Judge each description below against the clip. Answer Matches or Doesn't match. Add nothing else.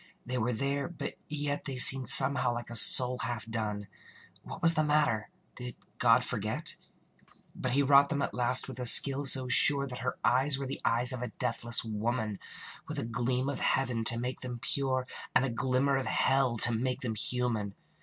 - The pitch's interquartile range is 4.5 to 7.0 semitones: Doesn't match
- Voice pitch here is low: Matches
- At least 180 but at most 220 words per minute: Matches